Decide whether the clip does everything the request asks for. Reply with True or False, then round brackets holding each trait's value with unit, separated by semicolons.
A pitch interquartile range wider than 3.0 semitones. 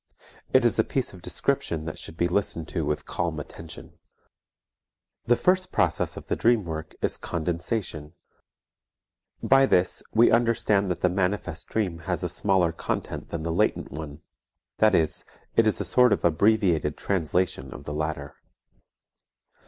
True (4.8 semitones)